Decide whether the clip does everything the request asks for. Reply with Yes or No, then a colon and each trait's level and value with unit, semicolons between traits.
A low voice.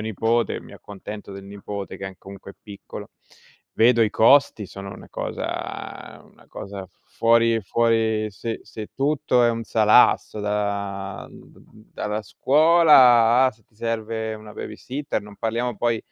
Yes: low, 110 Hz